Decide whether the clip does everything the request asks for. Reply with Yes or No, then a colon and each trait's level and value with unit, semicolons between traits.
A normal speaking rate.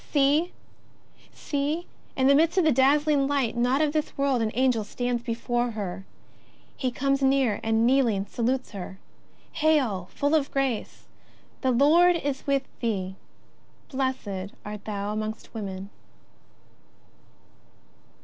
No: slow, 130 wpm